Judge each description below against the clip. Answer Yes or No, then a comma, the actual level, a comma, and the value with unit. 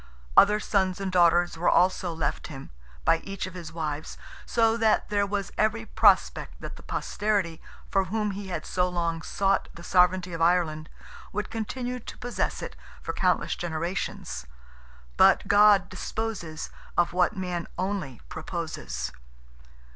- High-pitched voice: No, medium, 180 Hz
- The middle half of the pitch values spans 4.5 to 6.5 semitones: No, average, 3.5 semitones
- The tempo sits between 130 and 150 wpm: Yes, average, 145 wpm